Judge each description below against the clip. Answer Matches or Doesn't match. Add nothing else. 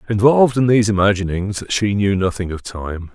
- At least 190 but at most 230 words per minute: Doesn't match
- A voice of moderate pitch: Doesn't match